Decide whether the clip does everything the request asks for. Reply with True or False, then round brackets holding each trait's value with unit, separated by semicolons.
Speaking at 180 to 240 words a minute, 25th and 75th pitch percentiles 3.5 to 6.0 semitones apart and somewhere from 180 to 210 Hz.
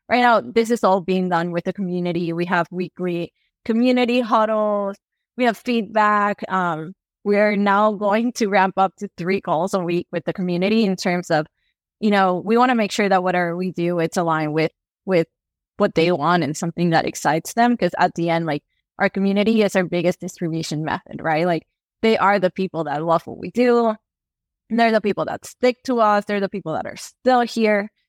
True (205 wpm; 3.8 semitones; 190 Hz)